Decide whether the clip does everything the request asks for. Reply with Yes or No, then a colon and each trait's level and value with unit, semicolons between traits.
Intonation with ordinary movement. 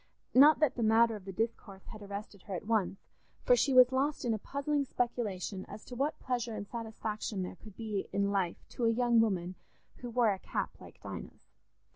Yes: average, 3.6 semitones